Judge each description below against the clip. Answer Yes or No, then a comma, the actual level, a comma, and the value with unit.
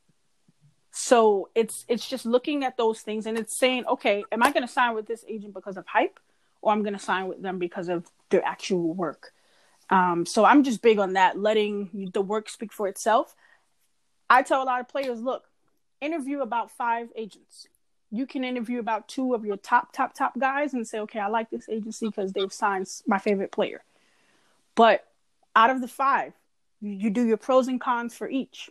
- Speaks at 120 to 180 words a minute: No, average, 200 wpm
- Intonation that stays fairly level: No, average, 3.6 semitones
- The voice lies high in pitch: Yes, high, 225 Hz